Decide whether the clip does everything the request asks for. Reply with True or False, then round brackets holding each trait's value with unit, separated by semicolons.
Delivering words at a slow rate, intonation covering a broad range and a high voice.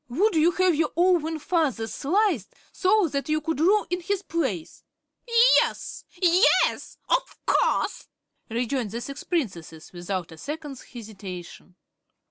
True (130 wpm; 8.0 semitones; 300 Hz)